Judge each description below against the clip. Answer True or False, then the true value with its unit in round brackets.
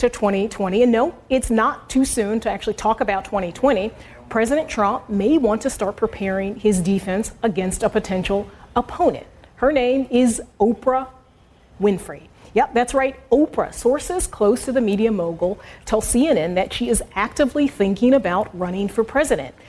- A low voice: False (225 Hz)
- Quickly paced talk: False (160 wpm)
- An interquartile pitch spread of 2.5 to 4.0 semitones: False (4.5 semitones)